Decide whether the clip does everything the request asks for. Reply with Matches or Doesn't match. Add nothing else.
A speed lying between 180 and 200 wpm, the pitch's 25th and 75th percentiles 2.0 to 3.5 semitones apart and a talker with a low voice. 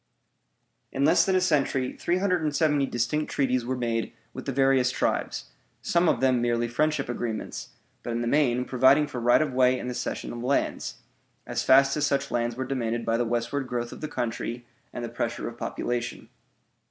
Matches